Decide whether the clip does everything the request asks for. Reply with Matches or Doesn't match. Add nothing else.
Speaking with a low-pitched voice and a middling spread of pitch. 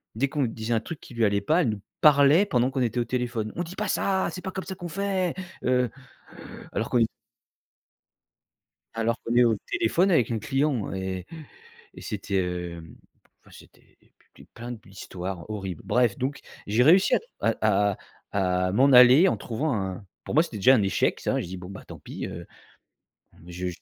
Doesn't match